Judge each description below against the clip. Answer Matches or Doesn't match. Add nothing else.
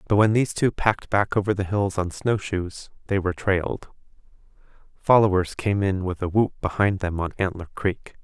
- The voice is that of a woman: Doesn't match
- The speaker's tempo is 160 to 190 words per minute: Matches